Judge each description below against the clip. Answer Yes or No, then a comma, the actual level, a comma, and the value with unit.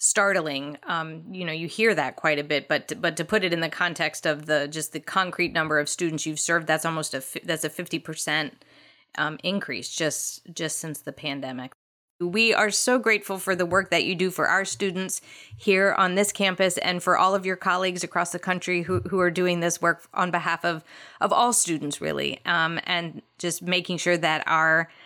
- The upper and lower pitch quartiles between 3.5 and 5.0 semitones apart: No, average, 3.0 semitones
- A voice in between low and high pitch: Yes, medium, 170 Hz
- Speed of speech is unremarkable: No, fast, 215 wpm